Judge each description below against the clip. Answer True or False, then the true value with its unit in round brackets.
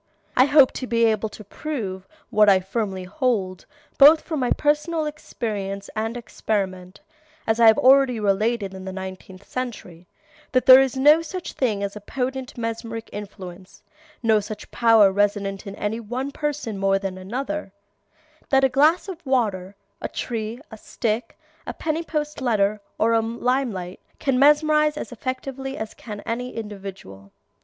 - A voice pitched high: True (225 Hz)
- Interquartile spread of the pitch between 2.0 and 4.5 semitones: False (5.1 semitones)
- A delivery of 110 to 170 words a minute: True (165 wpm)